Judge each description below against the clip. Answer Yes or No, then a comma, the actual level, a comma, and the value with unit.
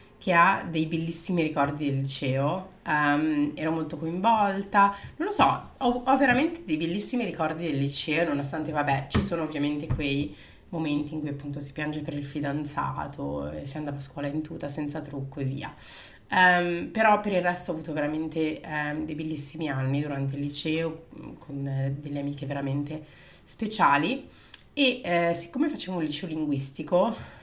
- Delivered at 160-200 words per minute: Yes, average, 165 wpm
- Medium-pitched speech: Yes, medium, 155 Hz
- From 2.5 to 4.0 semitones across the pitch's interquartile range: Yes, average, 3.0 semitones